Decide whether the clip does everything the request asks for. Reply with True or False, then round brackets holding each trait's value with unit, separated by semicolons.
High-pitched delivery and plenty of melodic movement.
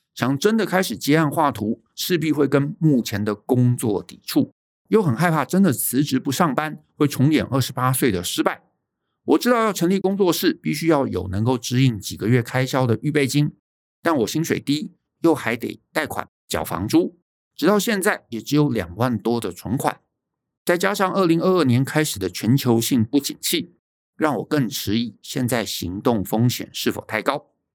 False (135 Hz; 5.7 semitones)